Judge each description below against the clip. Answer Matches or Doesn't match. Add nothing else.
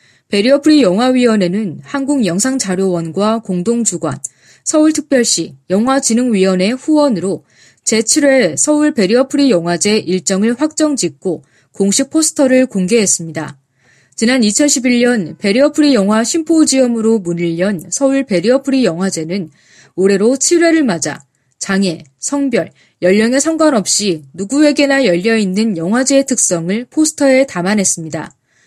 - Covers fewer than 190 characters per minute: Doesn't match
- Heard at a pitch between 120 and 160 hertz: Doesn't match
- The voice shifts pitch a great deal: Matches